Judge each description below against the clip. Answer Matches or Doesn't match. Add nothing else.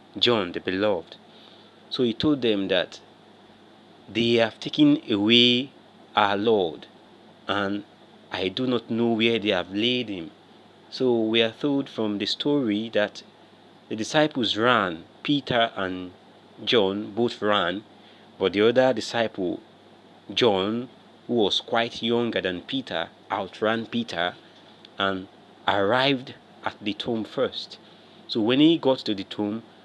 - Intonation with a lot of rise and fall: Doesn't match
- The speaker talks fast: Doesn't match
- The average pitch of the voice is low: Matches